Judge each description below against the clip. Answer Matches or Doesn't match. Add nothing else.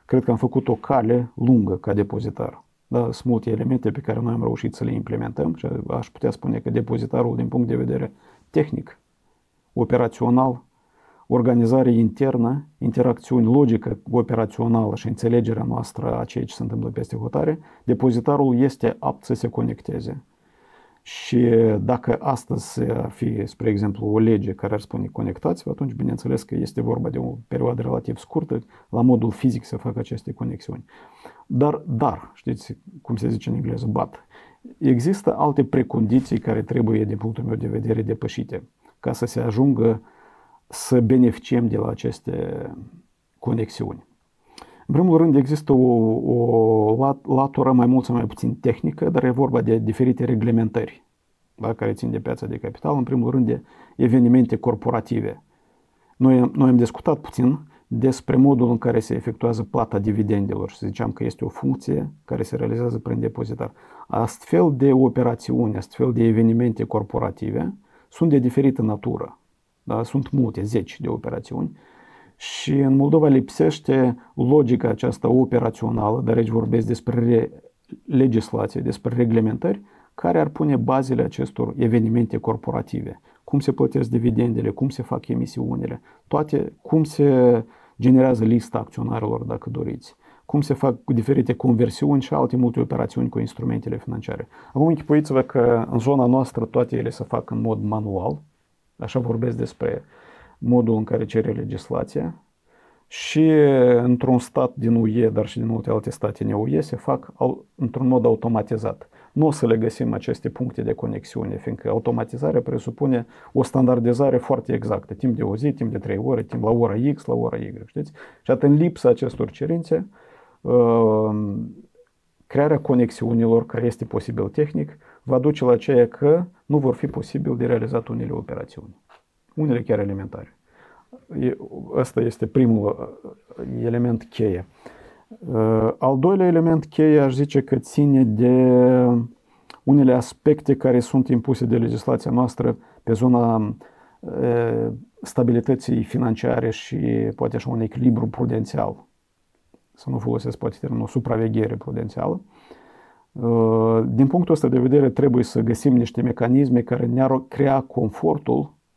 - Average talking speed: Matches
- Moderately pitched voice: Doesn't match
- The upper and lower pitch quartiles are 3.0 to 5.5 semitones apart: Doesn't match